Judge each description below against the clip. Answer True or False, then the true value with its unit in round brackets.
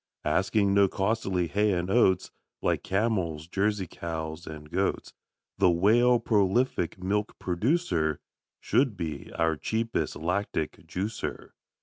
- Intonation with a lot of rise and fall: False (4.0 semitones)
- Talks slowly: True (115 wpm)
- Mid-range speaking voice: False (95 Hz)